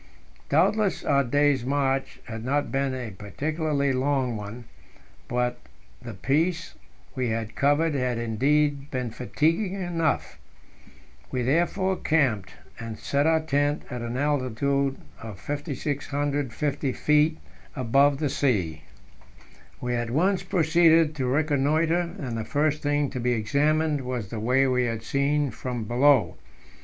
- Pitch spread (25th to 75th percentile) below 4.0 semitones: Yes, average, 3.5 semitones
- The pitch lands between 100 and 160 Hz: Yes, medium, 140 Hz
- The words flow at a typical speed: No, slow, 130 wpm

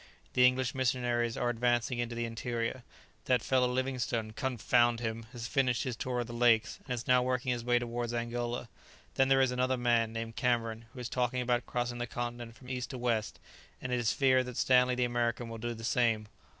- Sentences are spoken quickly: Yes, fast, 210 wpm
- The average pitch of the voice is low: Yes, low, 120 Hz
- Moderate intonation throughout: No, narrow, 1.3 semitones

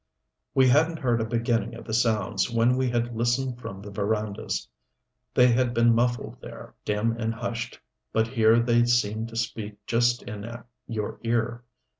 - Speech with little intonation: Yes, narrow, 1.4 semitones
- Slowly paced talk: No, average, 165 wpm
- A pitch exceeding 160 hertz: No, low, 115 Hz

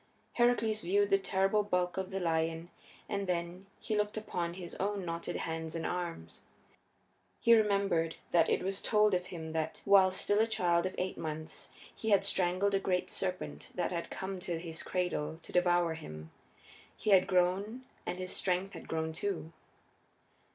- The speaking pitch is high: No, medium, 180 Hz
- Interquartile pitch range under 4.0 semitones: Yes, average, 2.8 semitones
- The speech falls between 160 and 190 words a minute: Yes, average, 170 wpm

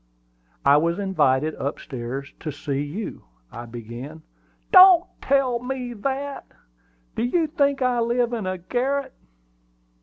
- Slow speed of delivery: Yes, slow, 130 wpm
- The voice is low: No, high, 220 Hz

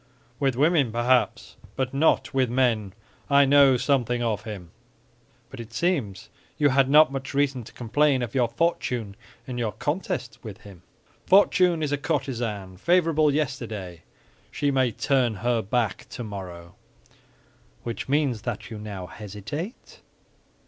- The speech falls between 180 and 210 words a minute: No, average, 140 wpm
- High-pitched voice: No, low, 125 Hz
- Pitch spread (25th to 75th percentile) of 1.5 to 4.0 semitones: No, average, 4.8 semitones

